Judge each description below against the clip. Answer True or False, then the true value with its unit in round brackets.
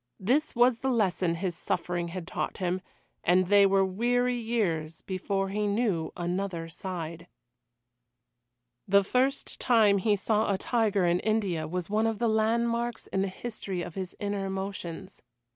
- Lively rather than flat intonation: False (3.8 semitones)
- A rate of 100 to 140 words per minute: False (155 wpm)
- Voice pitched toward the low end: False (195 Hz)